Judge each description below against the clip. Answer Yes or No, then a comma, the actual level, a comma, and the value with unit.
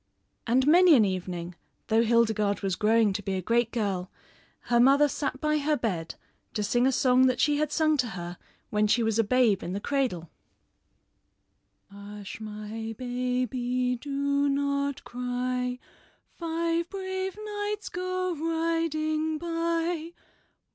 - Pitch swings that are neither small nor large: No, wide, 6.1 semitones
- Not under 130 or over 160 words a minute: Yes, average, 140 wpm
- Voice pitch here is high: Yes, very high, 255 Hz